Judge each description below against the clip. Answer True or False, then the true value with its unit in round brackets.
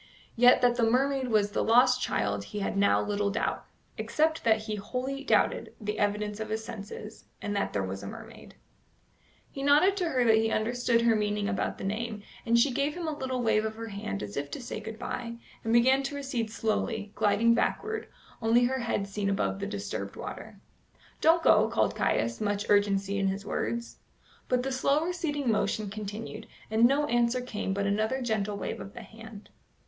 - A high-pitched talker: True (225 Hz)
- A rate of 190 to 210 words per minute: True (195 wpm)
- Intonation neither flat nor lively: True (3.4 semitones)